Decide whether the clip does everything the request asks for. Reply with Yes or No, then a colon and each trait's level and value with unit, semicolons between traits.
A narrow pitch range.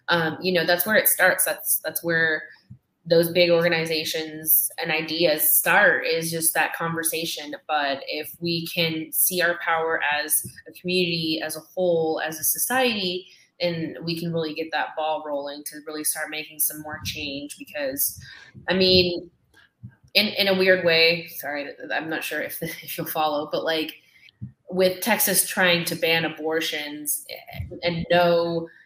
Yes: narrow, 1.9 semitones